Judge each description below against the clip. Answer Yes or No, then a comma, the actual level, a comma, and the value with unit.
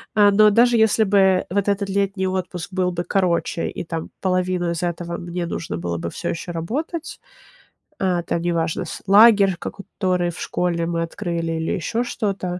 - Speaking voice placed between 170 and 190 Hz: Yes, medium, 185 Hz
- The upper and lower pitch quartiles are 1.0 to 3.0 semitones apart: Yes, average, 2.7 semitones